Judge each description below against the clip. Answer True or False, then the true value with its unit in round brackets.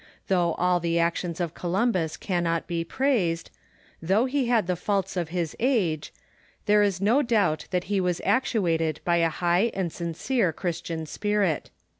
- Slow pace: False (160 wpm)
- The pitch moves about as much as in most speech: True (3.6 semitones)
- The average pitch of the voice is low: False (180 Hz)